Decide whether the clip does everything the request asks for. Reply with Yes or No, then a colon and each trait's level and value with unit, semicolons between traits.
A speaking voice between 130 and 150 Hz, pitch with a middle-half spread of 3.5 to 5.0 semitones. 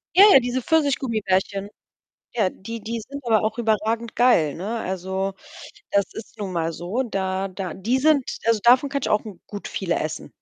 No: high, 215 Hz; average, 4.2 semitones